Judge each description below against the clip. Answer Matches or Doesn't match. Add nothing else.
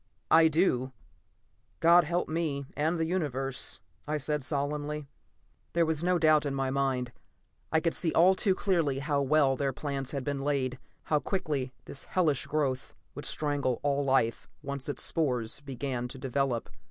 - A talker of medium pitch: Matches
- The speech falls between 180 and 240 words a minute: Doesn't match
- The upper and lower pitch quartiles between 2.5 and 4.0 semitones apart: Matches